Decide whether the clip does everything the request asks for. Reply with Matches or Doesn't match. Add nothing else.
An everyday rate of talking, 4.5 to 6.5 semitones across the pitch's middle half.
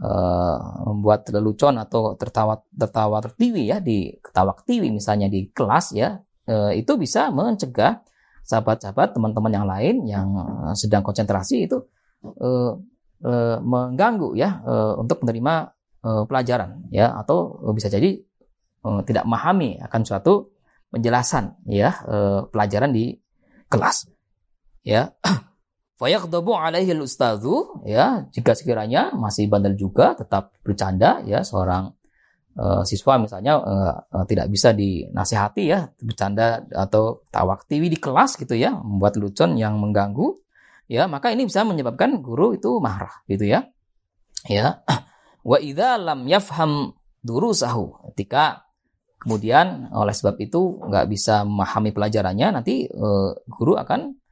Matches